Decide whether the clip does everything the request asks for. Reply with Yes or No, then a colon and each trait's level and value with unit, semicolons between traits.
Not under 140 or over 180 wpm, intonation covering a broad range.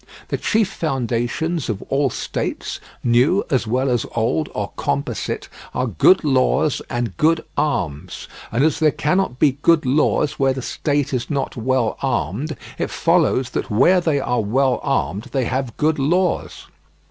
No: average, 160 wpm; average, 4.2 semitones